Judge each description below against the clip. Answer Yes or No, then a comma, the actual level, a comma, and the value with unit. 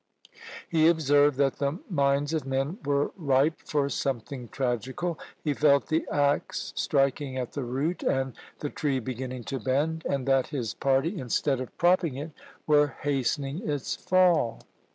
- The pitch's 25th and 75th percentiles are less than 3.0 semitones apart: Yes, narrow, 2.5 semitones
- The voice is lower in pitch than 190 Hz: Yes, medium, 140 Hz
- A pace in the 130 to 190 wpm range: Yes, average, 155 wpm